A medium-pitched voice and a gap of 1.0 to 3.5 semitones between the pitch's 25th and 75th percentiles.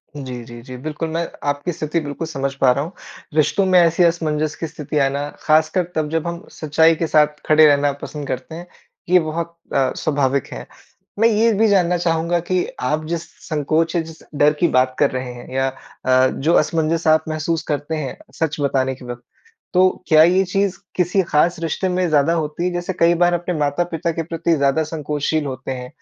Yes: medium, 155 Hz; average, 2.9 semitones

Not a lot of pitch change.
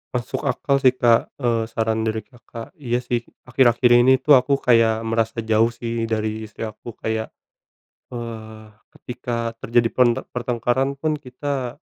Yes: narrow, 1.7 semitones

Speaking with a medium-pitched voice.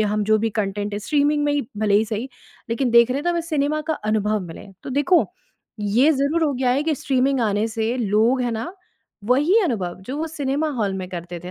No: high, 245 Hz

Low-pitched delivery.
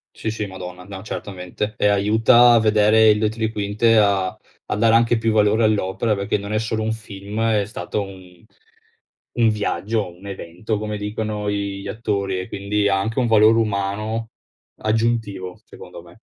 Yes: low, 105 Hz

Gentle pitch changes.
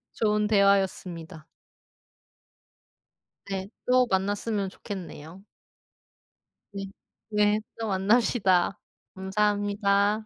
Yes: narrow, 1.7 semitones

